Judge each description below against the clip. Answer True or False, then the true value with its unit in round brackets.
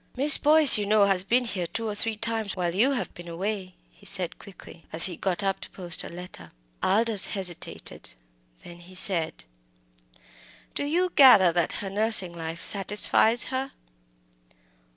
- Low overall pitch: False (195 Hz)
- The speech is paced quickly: False (165 wpm)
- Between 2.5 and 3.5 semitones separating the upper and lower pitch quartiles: False (4.3 semitones)